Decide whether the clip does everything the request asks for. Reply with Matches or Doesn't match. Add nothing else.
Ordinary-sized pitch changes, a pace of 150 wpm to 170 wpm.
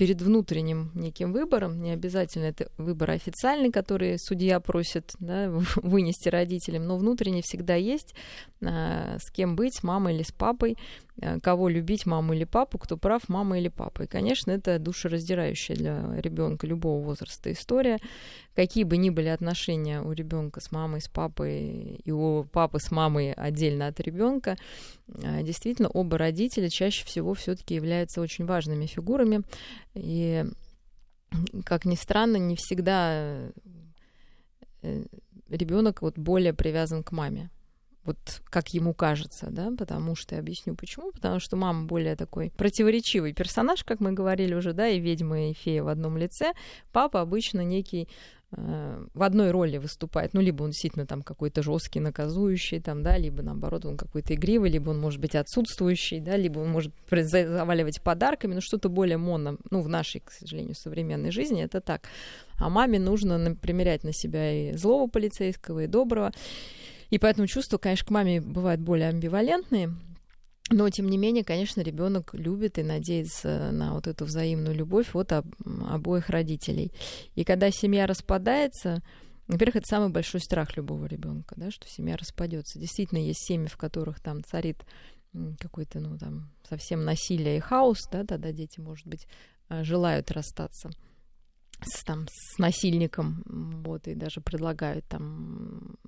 Matches